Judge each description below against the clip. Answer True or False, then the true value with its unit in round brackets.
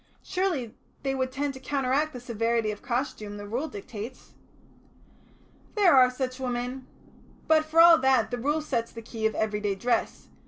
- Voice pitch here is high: True (255 Hz)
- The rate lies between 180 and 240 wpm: False (165 wpm)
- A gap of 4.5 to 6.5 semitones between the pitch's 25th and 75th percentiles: False (3.6 semitones)